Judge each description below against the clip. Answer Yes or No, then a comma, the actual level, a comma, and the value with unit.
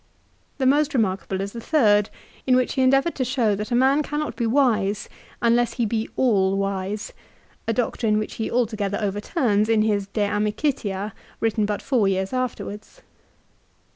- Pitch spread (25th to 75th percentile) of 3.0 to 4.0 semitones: Yes, average, 3.7 semitones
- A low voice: No, high, 220 Hz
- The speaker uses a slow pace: No, average, 170 wpm